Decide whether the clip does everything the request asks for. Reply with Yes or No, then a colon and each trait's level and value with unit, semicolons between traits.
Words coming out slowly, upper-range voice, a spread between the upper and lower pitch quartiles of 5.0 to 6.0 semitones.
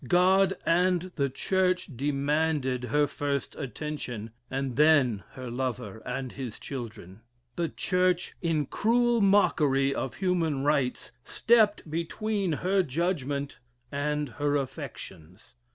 No: slow, 115 wpm; medium, 145 Hz; wide, 5.5 semitones